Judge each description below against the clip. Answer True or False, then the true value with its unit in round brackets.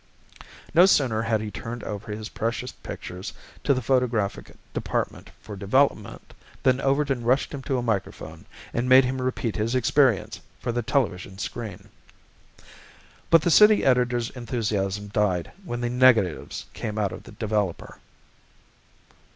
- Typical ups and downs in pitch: True (3.6 semitones)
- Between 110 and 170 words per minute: True (145 wpm)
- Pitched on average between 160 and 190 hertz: False (120 Hz)